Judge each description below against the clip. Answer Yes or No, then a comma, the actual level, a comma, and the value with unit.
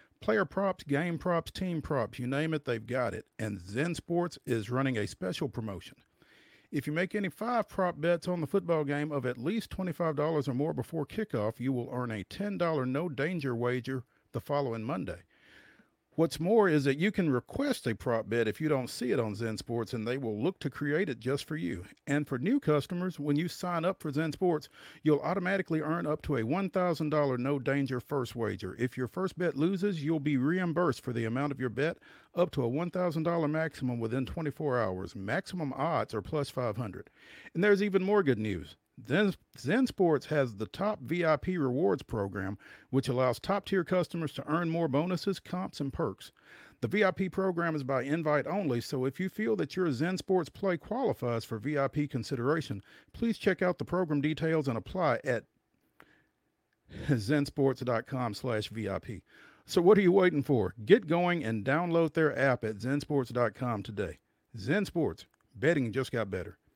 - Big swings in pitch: Yes, wide, 5.7 semitones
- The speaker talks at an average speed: Yes, average, 180 wpm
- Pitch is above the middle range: No, medium, 145 Hz